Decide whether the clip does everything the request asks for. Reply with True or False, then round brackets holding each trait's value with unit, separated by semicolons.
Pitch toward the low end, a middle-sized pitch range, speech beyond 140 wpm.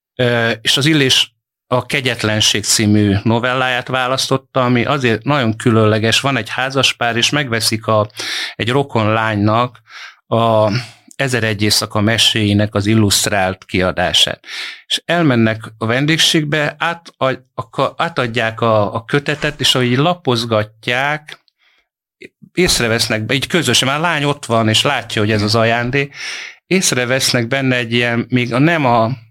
False (120 Hz; 3.5 semitones; 135 wpm)